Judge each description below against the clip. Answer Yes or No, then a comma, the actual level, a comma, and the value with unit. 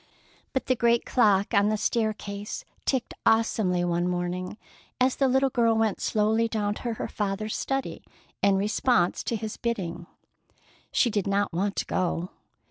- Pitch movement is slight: No, average, 3.3 semitones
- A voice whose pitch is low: No, high, 210 Hz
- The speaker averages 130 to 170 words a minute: Yes, average, 155 wpm